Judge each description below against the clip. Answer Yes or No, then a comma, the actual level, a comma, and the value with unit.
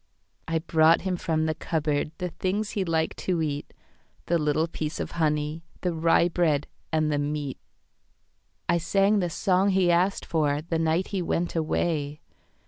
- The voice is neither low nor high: Yes, medium, 165 Hz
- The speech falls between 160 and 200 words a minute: No, average, 140 wpm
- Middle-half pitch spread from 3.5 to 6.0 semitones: No, narrow, 2.5 semitones